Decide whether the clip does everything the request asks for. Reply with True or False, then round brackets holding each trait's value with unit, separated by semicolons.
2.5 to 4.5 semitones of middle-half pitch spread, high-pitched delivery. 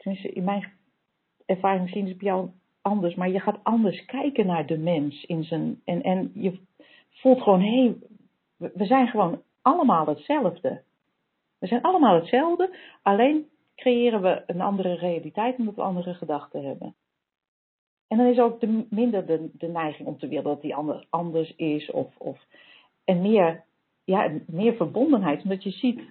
False (5.4 semitones; 195 Hz)